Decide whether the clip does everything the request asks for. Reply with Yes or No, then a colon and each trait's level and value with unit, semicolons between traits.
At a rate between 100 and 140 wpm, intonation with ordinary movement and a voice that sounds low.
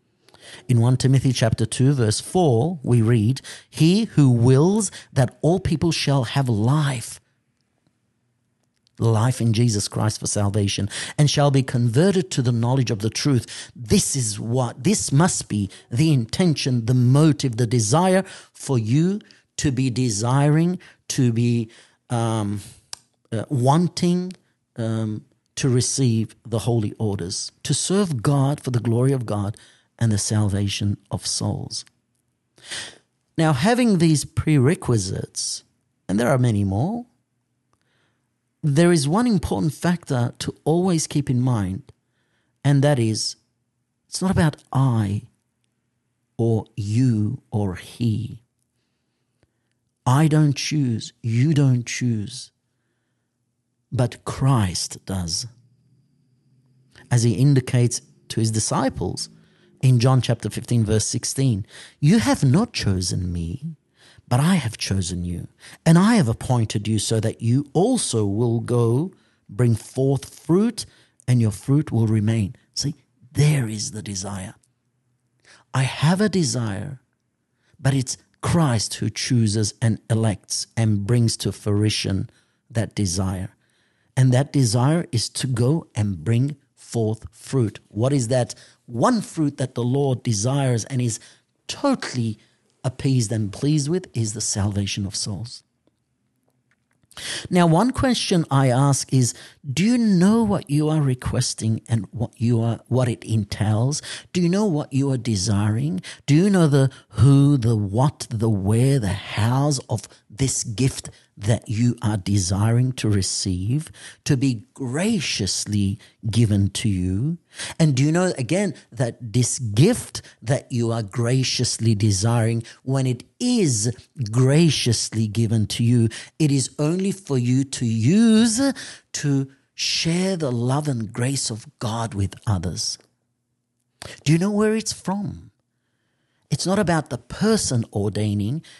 Yes: slow, 135 wpm; average, 4.0 semitones; low, 125 Hz